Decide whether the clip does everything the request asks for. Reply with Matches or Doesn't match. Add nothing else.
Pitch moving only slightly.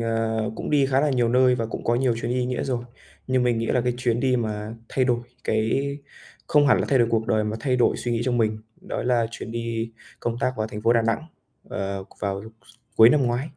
Matches